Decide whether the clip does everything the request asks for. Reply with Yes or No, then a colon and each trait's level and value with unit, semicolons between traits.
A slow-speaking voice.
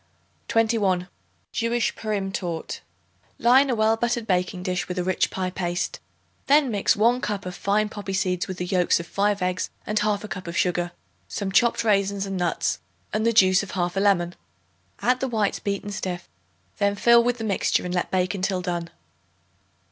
No: average, 180 wpm